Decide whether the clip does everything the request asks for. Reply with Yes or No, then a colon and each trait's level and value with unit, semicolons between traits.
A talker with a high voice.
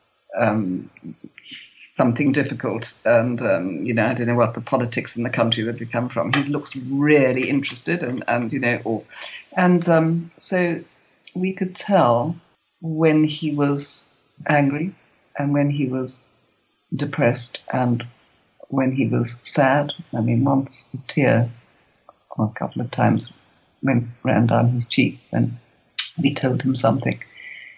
No: low, 135 Hz